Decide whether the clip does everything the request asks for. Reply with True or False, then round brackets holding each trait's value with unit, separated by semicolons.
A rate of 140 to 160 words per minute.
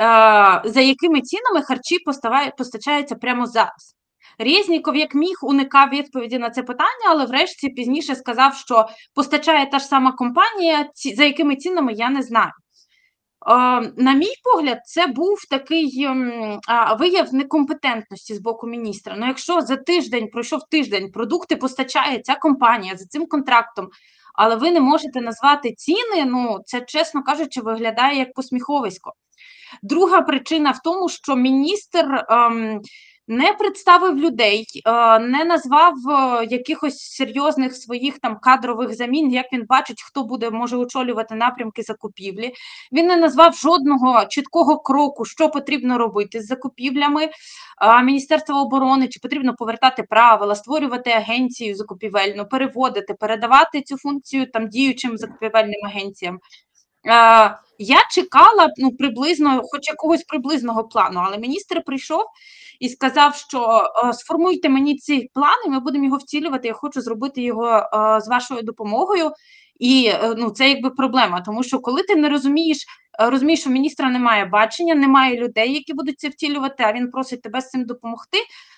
True (145 wpm)